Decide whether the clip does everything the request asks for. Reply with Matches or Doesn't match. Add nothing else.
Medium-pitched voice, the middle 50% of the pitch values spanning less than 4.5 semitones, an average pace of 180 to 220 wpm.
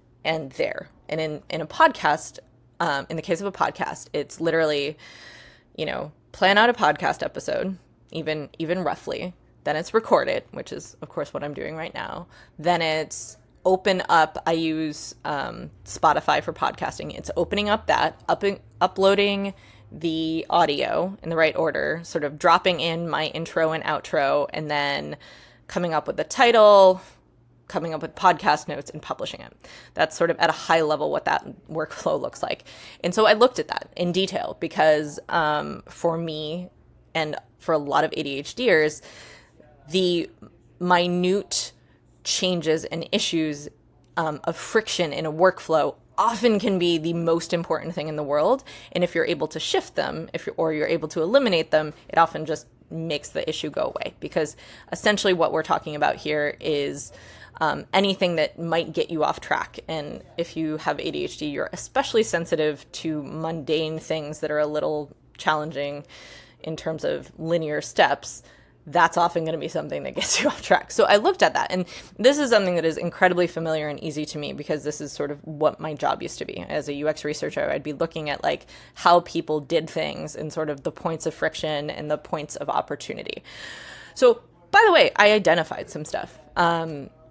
Matches